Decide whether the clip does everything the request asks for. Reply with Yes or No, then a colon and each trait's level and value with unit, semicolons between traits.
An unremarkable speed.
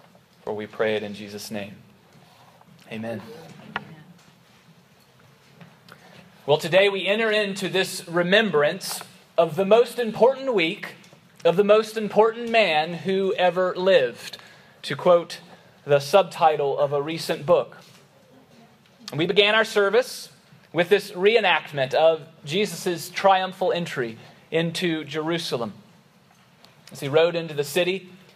No: slow, 115 wpm